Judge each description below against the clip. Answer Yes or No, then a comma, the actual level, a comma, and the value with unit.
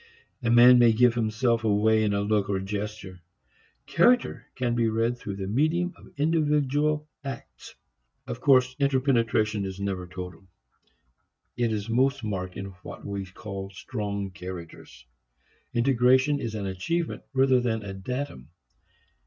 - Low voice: Yes, low, 115 Hz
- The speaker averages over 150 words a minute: No, average, 145 wpm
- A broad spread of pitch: No, average, 4.7 semitones